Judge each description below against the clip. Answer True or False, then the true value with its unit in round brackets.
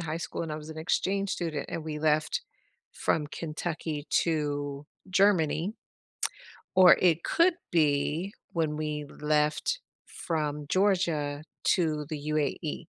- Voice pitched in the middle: True (155 Hz)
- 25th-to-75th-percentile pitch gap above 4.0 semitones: False (2.6 semitones)